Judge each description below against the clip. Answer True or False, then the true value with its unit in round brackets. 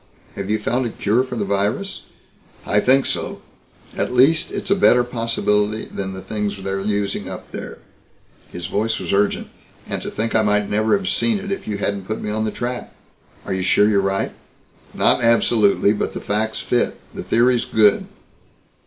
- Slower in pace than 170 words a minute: False (190 wpm)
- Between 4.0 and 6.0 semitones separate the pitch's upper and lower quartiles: False (3.2 semitones)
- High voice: False (110 Hz)